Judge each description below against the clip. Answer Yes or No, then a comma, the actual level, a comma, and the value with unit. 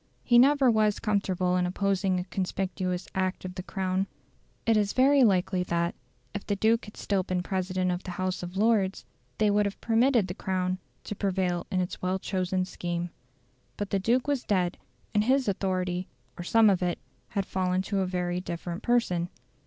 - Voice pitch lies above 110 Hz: Yes, high, 190 Hz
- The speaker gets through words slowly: No, average, 190 wpm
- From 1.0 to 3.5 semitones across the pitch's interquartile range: Yes, narrow, 2.4 semitones